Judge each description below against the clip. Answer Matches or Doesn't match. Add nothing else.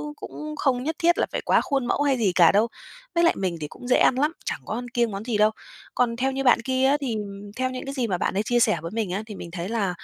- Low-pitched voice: Doesn't match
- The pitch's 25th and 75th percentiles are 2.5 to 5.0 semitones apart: Matches